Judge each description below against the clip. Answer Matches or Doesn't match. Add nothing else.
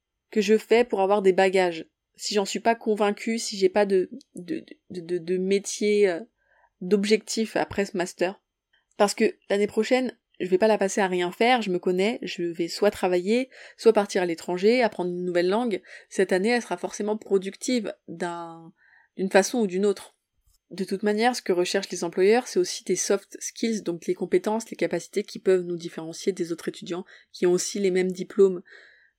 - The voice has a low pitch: Doesn't match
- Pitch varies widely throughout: Doesn't match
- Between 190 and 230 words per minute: Matches